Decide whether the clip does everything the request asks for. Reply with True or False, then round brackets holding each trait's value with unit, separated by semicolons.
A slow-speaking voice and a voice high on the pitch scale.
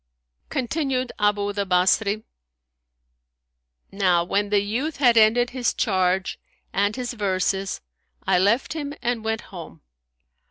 True (120 wpm; 210 Hz)